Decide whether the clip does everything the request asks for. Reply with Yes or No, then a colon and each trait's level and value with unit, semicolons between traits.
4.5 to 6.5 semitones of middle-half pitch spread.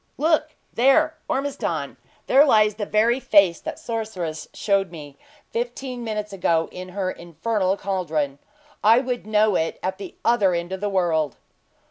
Yes: average, 4.8 semitones